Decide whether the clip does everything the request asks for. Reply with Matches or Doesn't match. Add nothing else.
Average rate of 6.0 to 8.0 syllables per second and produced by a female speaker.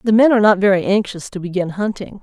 Matches